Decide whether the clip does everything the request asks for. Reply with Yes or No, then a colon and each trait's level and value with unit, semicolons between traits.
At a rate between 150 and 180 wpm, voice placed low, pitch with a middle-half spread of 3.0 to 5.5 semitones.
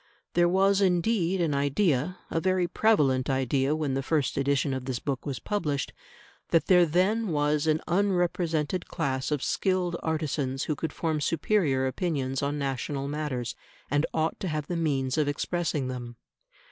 No: average, 160 wpm; medium, 150 Hz; average, 4.2 semitones